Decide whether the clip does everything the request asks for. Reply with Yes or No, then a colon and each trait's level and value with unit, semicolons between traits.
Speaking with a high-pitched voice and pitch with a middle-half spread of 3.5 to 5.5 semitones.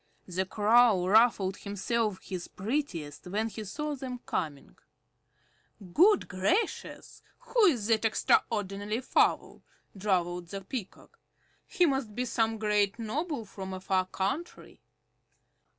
Yes: high, 210 Hz; average, 4.5 semitones